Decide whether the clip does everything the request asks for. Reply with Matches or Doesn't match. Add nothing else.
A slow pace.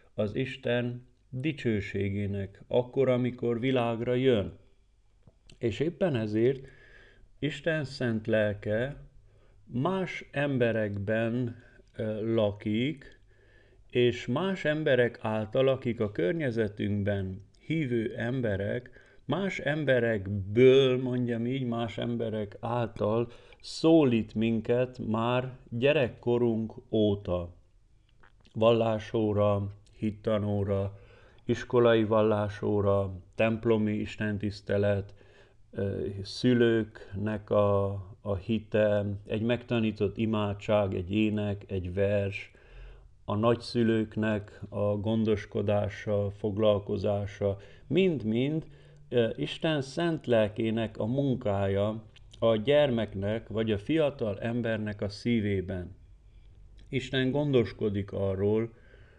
Matches